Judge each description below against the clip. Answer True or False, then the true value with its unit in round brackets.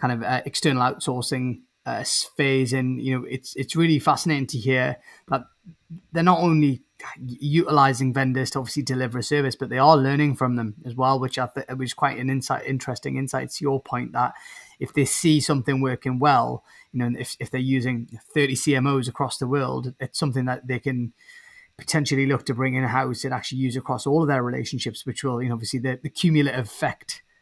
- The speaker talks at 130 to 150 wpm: False (205 wpm)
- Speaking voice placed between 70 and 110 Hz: False (130 Hz)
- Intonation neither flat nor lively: False (2.1 semitones)